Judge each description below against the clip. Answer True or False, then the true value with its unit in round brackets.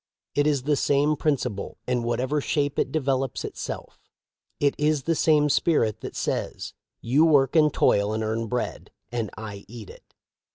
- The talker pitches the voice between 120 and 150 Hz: True (135 Hz)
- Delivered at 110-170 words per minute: True (165 wpm)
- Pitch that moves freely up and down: False (4.3 semitones)